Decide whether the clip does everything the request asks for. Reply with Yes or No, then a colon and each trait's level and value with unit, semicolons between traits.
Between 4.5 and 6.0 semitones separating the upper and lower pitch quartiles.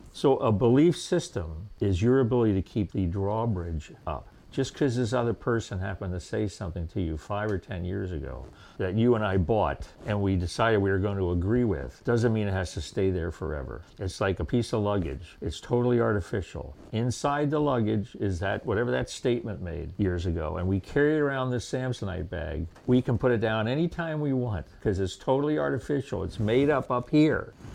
Yes: average, 5.1 semitones